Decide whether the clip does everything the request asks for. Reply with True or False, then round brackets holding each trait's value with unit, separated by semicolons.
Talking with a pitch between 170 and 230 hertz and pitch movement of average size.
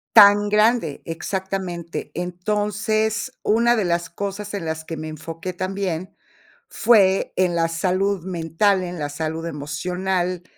True (185 Hz; 3.5 semitones)